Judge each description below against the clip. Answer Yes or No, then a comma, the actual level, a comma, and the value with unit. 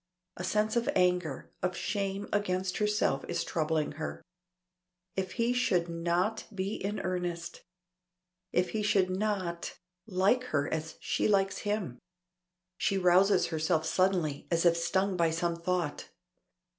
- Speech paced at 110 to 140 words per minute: Yes, slow, 135 wpm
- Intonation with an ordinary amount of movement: Yes, average, 3.0 semitones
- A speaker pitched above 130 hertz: Yes, medium, 185 Hz